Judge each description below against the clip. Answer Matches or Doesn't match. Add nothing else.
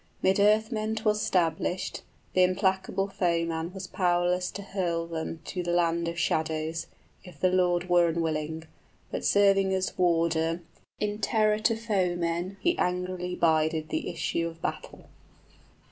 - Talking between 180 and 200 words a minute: Doesn't match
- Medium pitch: Matches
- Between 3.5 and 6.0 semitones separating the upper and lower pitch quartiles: Doesn't match